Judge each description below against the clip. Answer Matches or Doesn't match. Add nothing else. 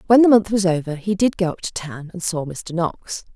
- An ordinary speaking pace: Doesn't match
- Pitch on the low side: Doesn't match